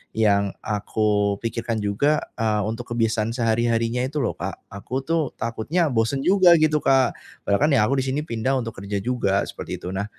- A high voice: No, low, 115 Hz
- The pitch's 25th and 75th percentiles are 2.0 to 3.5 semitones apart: No, average, 4.1 semitones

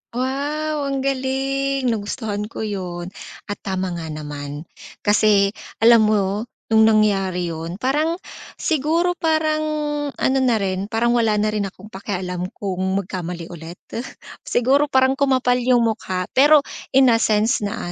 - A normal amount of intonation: No, wide, 5.9 semitones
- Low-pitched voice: No, high, 220 Hz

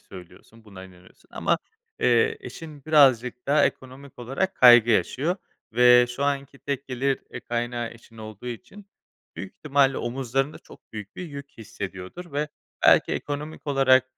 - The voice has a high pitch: No, low, 130 Hz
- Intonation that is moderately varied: Yes, average, 3.4 semitones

